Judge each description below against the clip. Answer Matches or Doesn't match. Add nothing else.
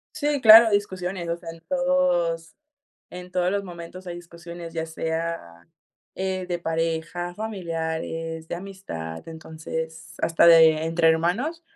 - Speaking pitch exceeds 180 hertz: Doesn't match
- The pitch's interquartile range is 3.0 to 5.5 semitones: Doesn't match